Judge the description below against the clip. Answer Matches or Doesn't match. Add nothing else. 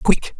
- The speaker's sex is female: Doesn't match